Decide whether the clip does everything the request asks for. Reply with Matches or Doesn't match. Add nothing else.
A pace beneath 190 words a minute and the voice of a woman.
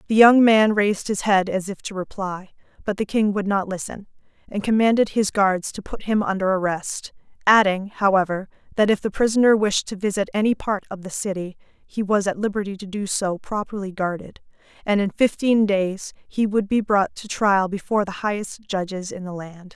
Doesn't match